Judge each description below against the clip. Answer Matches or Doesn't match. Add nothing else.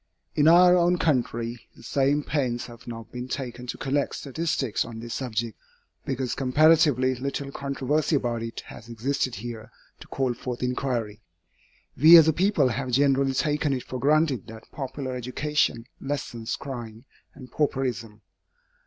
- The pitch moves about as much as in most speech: Matches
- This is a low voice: Matches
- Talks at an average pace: Matches